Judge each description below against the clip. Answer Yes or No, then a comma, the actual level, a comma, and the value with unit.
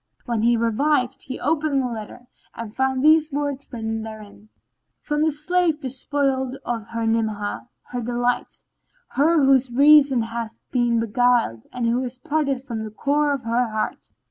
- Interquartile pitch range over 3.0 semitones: Yes, average, 3.7 semitones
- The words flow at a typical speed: Yes, average, 160 wpm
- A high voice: Yes, very high, 250 Hz